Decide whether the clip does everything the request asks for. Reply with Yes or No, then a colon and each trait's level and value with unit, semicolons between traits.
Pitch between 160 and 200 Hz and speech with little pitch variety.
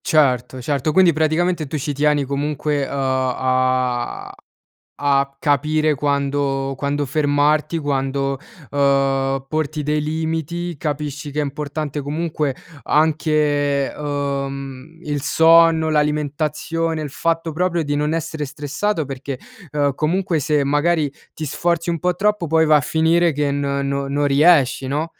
No: medium, 145 Hz; narrow, 2.3 semitones